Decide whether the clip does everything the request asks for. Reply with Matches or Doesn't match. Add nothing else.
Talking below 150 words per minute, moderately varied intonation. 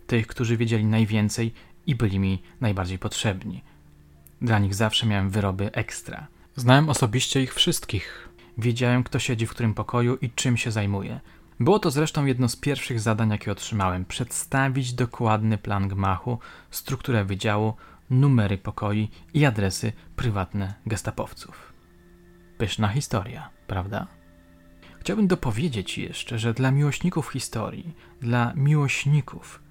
Matches